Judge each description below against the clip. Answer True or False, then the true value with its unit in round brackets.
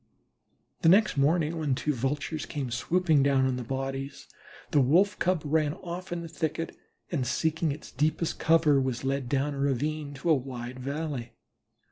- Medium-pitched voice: True (145 Hz)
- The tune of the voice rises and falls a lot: False (3.2 semitones)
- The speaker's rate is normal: True (170 wpm)